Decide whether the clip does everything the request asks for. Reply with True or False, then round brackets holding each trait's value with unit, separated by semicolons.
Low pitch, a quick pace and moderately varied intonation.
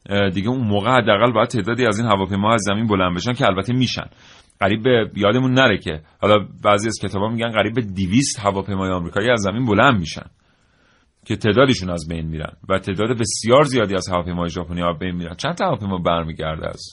True (100 Hz; 200 wpm; 4.7 semitones)